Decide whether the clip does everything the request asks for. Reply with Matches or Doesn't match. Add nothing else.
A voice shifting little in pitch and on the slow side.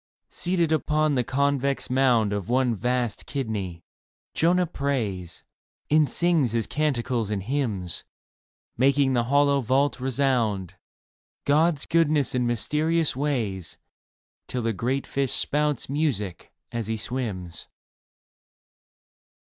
Doesn't match